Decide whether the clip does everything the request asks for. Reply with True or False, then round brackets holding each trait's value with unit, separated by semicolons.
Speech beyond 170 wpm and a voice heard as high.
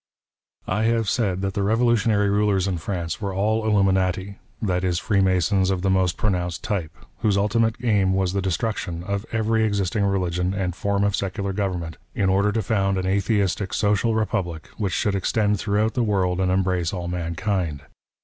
False (180 wpm; 100 Hz)